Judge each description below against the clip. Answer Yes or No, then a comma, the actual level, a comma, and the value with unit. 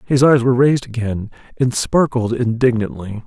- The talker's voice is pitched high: No, low, 120 Hz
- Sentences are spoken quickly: No, average, 145 wpm